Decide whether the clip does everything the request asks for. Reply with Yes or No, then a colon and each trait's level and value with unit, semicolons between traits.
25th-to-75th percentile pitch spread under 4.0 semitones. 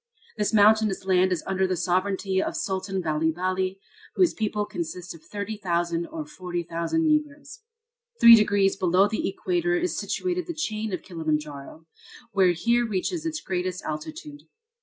No: average, 4.6 semitones